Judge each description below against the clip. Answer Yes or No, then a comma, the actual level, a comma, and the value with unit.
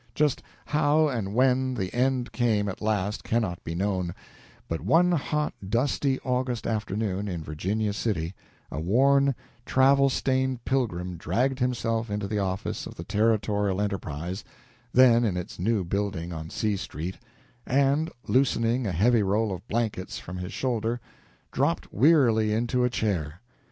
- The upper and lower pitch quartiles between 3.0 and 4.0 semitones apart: No, average, 5.1 semitones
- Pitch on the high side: No, low, 110 Hz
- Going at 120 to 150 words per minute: Yes, average, 145 wpm